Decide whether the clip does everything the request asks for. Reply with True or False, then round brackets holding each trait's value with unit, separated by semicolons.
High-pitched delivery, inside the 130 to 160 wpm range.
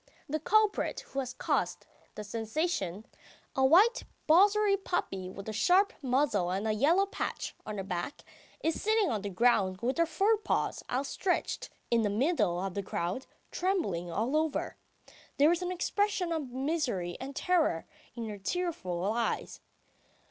True (265 Hz; 155 wpm)